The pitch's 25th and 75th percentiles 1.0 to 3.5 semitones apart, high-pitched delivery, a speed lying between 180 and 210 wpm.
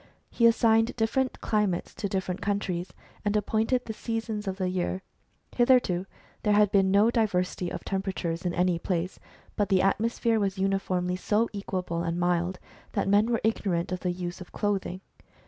No: average, 3.2 semitones; high, 195 Hz; average, 170 wpm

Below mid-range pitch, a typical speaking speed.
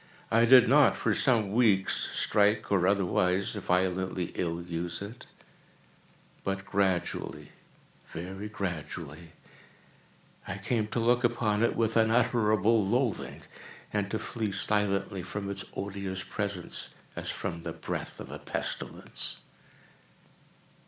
No: low, 100 Hz; slow, 110 wpm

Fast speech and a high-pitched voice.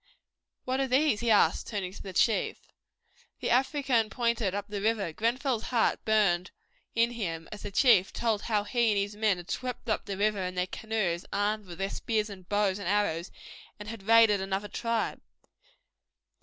No: average, 185 wpm; high, 210 Hz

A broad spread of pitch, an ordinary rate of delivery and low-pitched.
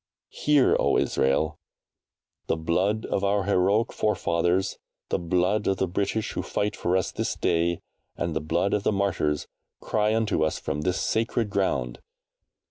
No: average, 3.6 semitones; average, 155 wpm; very low, 95 Hz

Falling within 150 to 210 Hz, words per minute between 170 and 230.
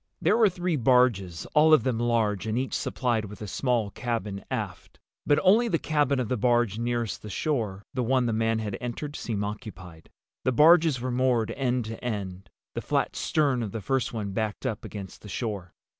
No: low, 120 Hz; average, 190 wpm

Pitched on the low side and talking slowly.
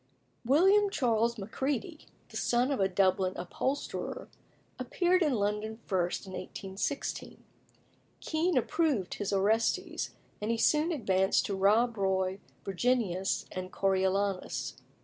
No: high, 220 Hz; slow, 115 wpm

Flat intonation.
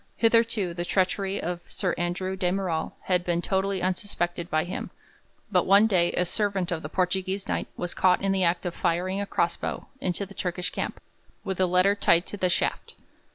Yes: narrow, 2.0 semitones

